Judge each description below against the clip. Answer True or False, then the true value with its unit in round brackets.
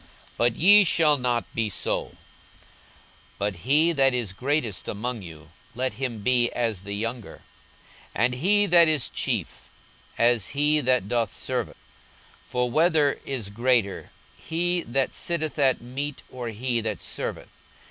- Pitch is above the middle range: False (125 Hz)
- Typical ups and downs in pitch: True (4.6 semitones)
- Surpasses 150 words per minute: False (145 wpm)